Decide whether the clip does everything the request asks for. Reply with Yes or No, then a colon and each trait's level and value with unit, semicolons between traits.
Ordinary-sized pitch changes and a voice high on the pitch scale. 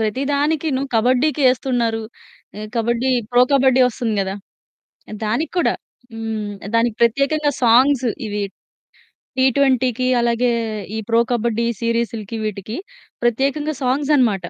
Yes: average, 3.2 semitones; high, 240 Hz